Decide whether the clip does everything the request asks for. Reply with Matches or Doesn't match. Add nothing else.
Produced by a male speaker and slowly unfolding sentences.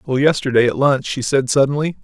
Doesn't match